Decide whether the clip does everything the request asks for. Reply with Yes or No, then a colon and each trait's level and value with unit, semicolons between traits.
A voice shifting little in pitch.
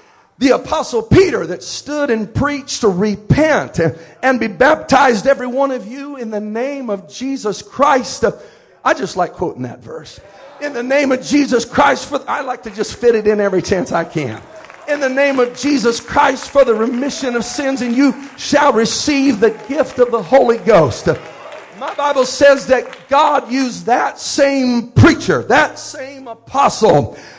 No: average, 3.3 semitones